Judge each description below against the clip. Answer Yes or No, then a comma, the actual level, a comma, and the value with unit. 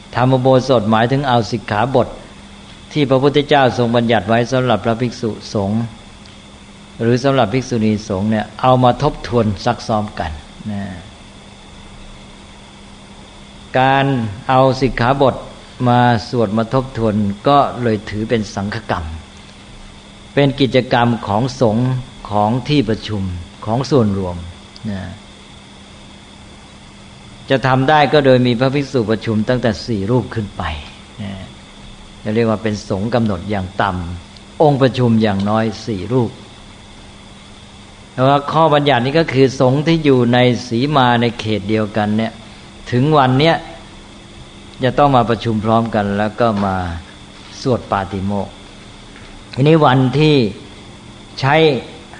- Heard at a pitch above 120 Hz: No, low, 110 Hz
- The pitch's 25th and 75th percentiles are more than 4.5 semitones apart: No, average, 4.0 semitones